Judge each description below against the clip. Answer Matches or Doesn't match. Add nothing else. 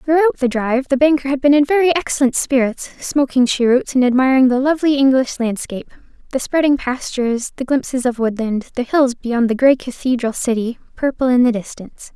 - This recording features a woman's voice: Matches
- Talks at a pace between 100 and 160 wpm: Doesn't match